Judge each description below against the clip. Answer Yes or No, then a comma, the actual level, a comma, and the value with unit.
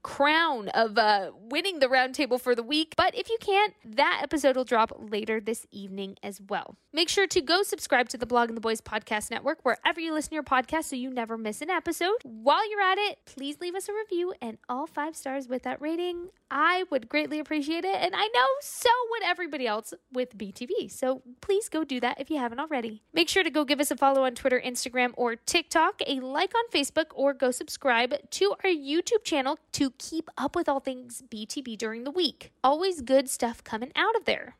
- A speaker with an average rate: No, fast, 220 wpm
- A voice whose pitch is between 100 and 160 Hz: No, very high, 285 Hz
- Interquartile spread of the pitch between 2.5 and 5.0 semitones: No, wide, 5.6 semitones